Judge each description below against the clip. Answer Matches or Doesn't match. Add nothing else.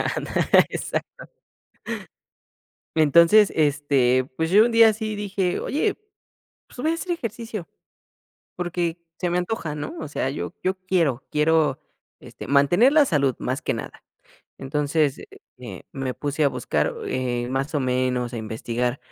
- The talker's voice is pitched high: Doesn't match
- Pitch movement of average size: Doesn't match